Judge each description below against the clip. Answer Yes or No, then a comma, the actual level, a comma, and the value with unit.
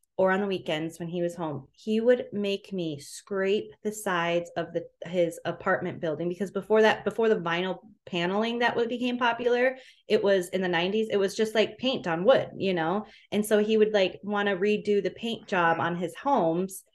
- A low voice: No, high, 195 Hz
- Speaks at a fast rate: Yes, fast, 210 wpm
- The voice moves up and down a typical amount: Yes, average, 3.8 semitones